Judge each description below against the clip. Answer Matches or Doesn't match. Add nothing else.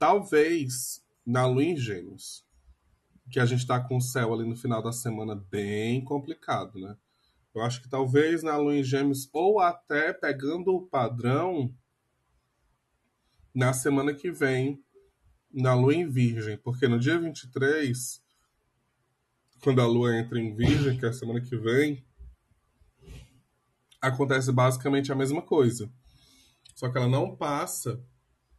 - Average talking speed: Matches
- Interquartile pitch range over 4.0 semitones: Doesn't match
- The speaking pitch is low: Matches